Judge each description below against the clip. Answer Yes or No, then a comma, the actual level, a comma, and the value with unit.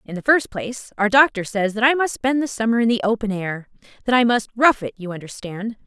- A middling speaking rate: No, fast, 235 wpm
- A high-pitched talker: Yes, high, 220 Hz